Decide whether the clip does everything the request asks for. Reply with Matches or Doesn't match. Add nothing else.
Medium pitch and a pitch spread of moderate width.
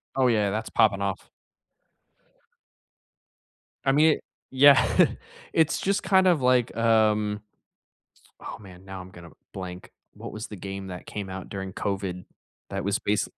Doesn't match